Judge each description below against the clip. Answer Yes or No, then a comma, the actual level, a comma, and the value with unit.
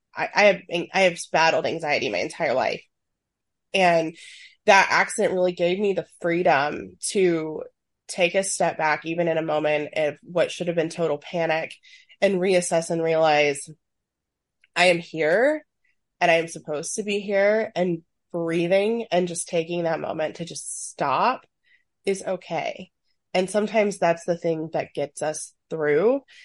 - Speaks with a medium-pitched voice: Yes, medium, 175 Hz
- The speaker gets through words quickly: No, average, 155 wpm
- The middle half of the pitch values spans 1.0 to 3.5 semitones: Yes, average, 3.2 semitones